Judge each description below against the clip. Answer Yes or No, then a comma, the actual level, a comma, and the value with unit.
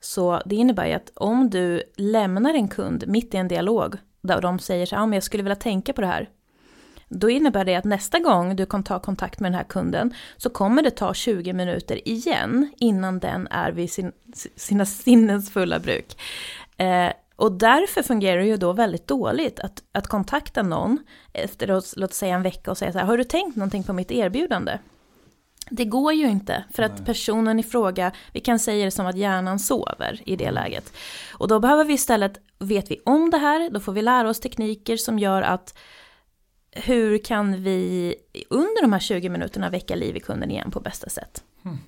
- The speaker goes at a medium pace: No, fast, 205 wpm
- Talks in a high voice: Yes, high, 210 Hz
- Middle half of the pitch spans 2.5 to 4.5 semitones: Yes, average, 4.2 semitones